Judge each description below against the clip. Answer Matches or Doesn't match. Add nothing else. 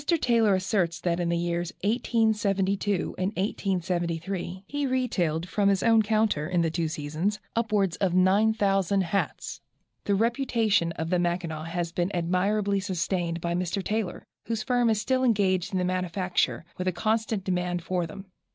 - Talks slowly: Doesn't match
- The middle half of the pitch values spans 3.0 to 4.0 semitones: Matches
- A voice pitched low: Doesn't match